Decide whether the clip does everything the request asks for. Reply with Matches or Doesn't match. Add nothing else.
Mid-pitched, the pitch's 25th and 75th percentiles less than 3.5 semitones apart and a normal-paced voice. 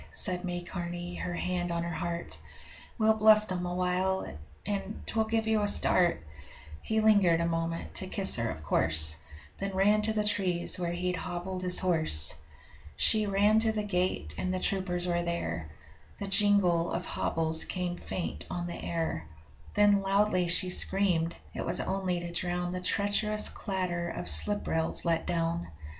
Matches